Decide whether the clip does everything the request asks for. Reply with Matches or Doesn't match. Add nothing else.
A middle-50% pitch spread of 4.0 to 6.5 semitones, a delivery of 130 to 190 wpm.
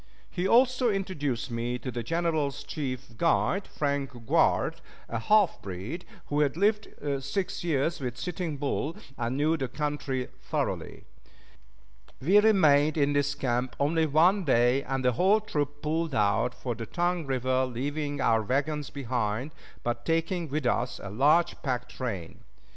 Matches